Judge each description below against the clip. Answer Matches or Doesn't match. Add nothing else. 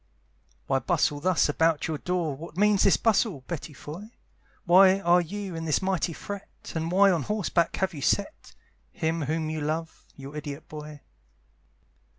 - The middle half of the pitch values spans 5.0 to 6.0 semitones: Doesn't match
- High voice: Doesn't match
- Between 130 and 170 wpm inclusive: Matches